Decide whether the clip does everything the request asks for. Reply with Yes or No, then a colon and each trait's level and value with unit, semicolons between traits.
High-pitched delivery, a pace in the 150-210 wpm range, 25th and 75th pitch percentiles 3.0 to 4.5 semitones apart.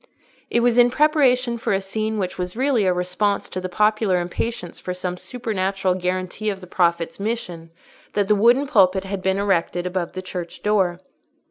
Yes: high, 195 Hz; average, 180 wpm; average, 3.4 semitones